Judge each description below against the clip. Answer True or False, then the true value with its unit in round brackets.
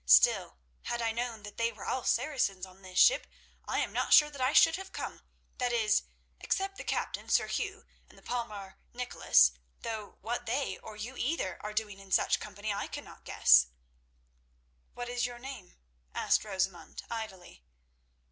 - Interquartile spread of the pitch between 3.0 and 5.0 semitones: True (4.1 semitones)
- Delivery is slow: False (170 wpm)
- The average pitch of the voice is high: True (225 Hz)